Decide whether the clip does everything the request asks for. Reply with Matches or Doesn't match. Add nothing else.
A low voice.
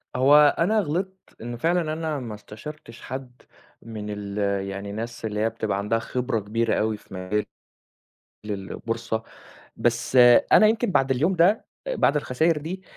Matches